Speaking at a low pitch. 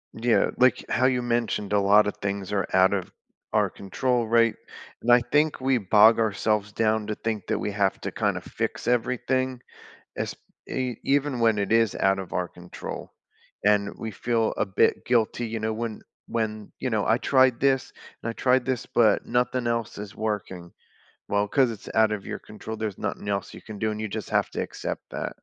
Yes: low, 110 Hz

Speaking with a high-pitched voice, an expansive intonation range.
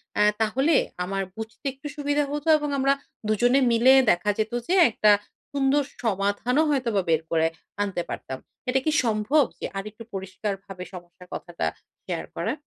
Yes: high, 220 Hz; wide, 5.8 semitones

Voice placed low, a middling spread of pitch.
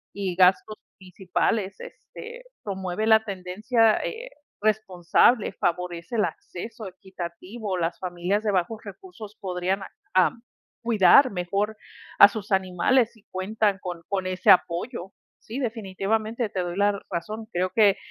No: high, 195 Hz; average, 3.2 semitones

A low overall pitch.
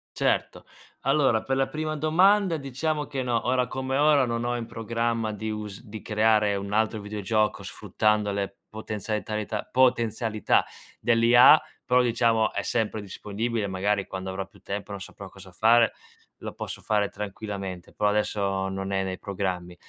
Yes: low, 110 Hz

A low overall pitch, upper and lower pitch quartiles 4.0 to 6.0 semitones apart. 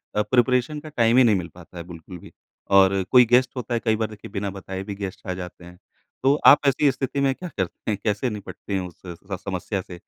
Yes: low, 105 Hz; average, 5.1 semitones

